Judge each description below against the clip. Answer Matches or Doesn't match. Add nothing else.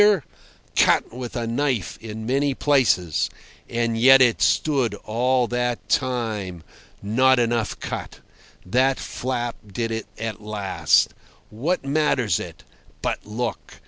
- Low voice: Matches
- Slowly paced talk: Matches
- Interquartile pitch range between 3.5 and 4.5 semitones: Doesn't match